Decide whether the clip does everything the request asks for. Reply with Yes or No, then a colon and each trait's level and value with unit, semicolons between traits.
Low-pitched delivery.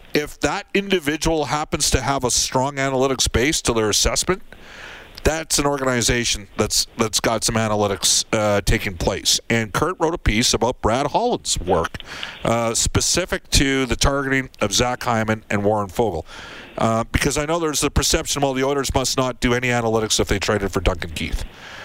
Yes: low, 125 Hz